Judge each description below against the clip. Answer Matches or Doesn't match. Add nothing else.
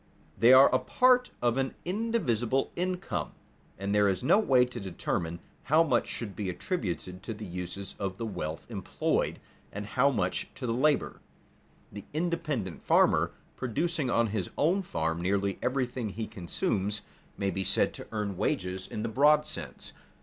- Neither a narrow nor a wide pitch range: Doesn't match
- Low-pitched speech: Matches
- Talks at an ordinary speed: Matches